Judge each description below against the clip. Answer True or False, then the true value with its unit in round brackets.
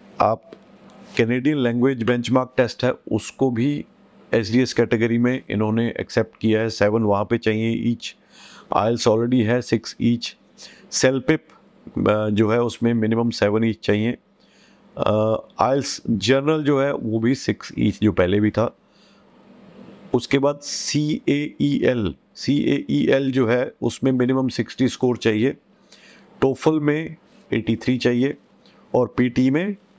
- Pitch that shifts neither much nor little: True (3.2 semitones)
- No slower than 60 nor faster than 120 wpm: False (140 wpm)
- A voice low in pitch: True (120 Hz)